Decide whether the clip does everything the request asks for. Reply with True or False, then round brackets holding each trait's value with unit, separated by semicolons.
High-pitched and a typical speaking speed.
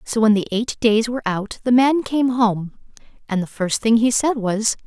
False (225 Hz; 220 wpm)